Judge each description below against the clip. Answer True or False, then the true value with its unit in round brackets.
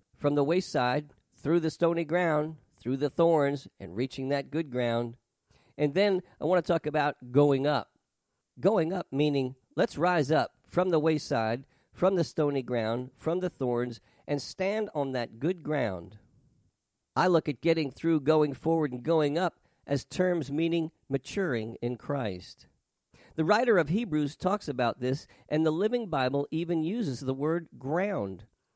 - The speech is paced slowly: False (165 wpm)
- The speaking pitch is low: False (145 Hz)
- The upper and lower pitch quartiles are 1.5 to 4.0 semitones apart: False (4.5 semitones)